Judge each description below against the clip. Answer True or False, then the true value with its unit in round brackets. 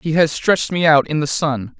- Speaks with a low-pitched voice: False (155 Hz)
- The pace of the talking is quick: True (270 wpm)